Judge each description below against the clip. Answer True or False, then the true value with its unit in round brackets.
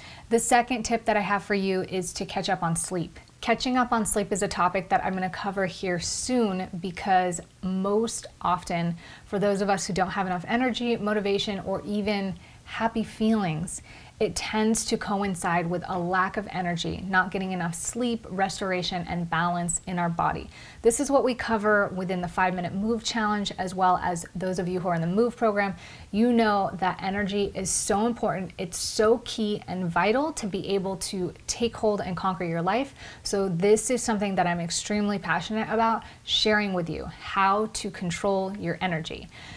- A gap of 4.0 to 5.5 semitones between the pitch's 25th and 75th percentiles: False (2.9 semitones)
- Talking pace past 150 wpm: True (190 wpm)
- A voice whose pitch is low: False (195 Hz)